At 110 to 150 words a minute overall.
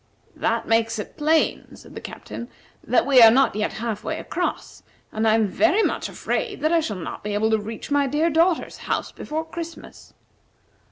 No: average, 190 wpm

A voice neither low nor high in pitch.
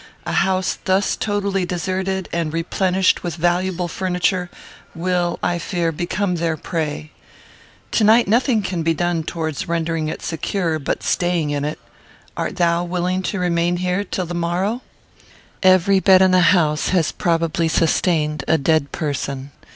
Yes: medium, 175 Hz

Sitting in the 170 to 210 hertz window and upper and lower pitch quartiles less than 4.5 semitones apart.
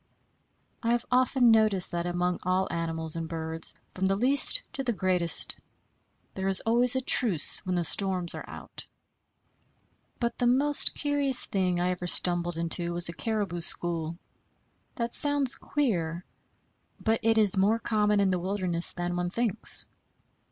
No: high, 190 Hz; average, 5.1 semitones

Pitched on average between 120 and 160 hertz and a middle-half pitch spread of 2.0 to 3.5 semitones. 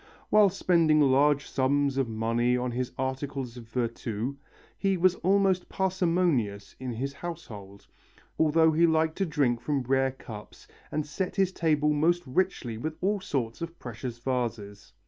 No: medium, 140 Hz; wide, 5.6 semitones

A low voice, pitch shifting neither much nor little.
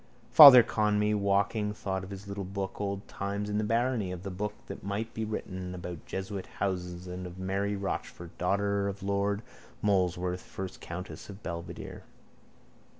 No: low, 100 Hz; narrow, 2.0 semitones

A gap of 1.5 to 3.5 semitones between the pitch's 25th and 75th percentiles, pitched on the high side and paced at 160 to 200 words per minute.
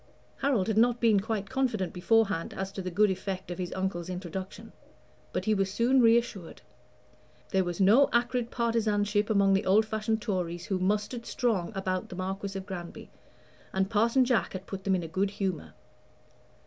Yes: average, 3.1 semitones; high, 195 Hz; average, 175 wpm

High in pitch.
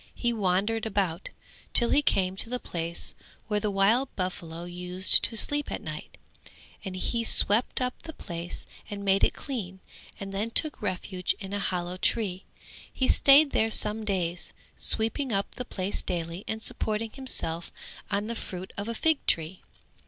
Yes: high, 200 Hz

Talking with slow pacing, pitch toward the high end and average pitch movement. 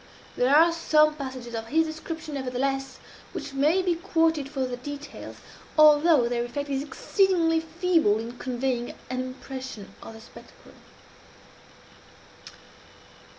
Yes: slow, 125 wpm; very high, 275 Hz; average, 4.2 semitones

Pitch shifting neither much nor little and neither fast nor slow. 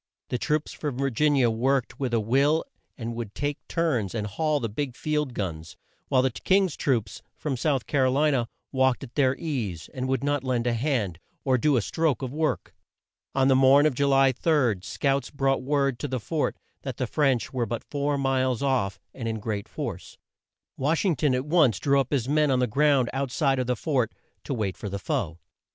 No: average, 3.4 semitones; fast, 220 wpm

